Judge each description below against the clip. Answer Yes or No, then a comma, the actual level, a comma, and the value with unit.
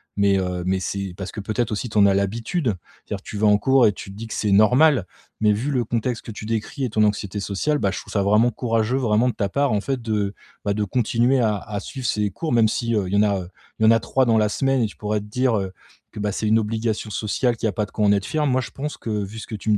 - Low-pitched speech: Yes, low, 110 Hz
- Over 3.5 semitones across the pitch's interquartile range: No, average, 2.9 semitones